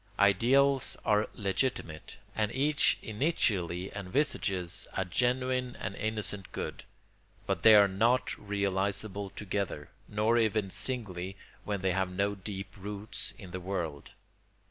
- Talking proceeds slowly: Yes, slow, 120 wpm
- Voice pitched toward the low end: Yes, low, 100 Hz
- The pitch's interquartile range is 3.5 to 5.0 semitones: No, average, 2.8 semitones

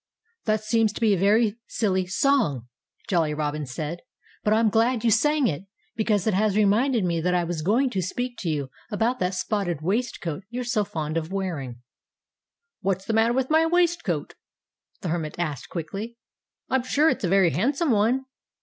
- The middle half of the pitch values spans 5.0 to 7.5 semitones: Yes, wide, 5.6 semitones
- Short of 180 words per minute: No, average, 185 wpm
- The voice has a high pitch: Yes, high, 205 Hz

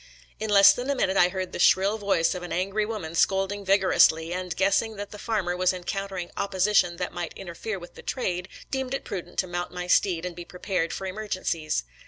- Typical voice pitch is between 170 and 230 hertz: Yes, high, 190 Hz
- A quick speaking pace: Yes, fast, 215 wpm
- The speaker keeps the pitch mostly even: Yes, narrow, 2.3 semitones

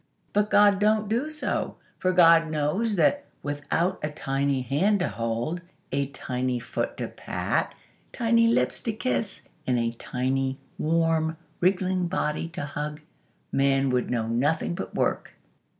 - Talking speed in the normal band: Yes, average, 145 wpm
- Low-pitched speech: No, medium, 160 Hz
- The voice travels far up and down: Yes, wide, 6.3 semitones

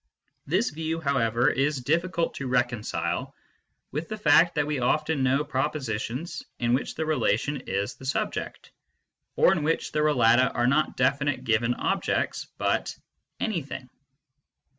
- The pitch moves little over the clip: No, average, 3.8 semitones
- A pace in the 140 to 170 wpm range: Yes, average, 145 wpm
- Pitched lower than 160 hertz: Yes, medium, 140 Hz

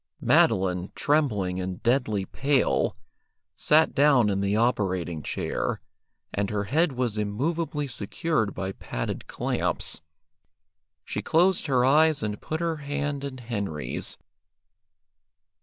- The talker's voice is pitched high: No, low, 120 Hz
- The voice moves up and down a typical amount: No, wide, 6.7 semitones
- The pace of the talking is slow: Yes, slow, 115 wpm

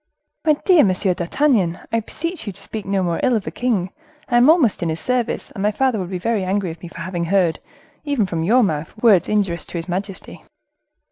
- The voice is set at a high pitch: Yes, high, 195 Hz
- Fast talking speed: Yes, fast, 220 wpm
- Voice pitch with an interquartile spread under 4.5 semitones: No, average, 5.3 semitones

